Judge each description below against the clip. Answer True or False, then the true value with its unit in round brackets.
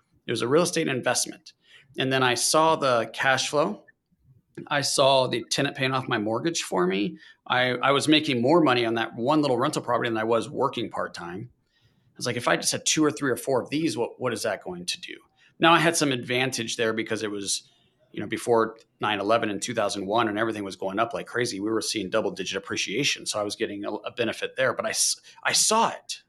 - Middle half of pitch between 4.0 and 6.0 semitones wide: True (4.7 semitones)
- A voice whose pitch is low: True (130 Hz)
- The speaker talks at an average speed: False (235 wpm)